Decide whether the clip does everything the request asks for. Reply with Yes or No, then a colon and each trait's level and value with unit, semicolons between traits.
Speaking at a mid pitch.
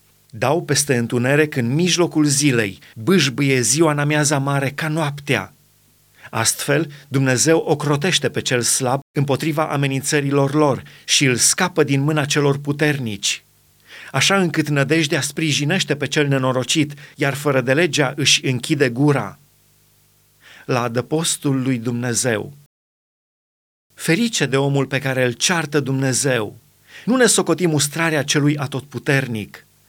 Yes: medium, 145 Hz